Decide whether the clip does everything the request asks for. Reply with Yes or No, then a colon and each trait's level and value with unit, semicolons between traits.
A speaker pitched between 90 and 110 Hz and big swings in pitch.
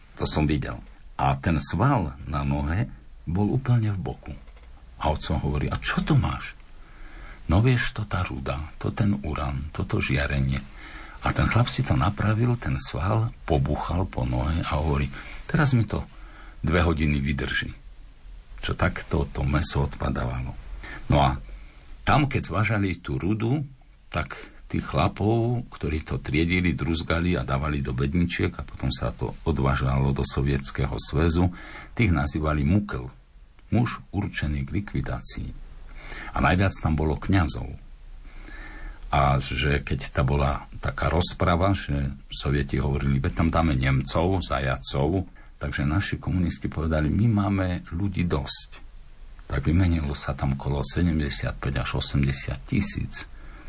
No: very low, 75 Hz; wide, 5.7 semitones